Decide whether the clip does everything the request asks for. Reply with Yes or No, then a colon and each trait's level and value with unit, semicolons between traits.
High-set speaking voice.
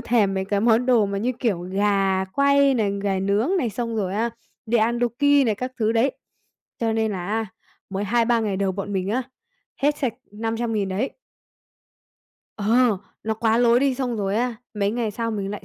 Yes: high, 220 Hz